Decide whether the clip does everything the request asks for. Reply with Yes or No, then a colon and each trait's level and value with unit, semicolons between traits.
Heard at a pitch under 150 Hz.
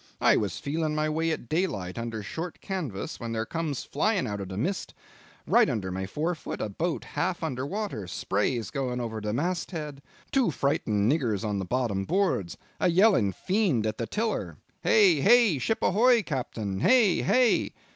Yes: medium, 140 Hz